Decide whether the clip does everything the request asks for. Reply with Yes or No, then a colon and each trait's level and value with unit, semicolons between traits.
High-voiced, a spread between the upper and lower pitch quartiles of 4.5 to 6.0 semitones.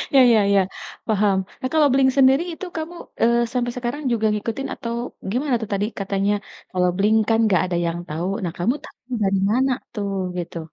Yes: high, 225 Hz; average, 4.9 semitones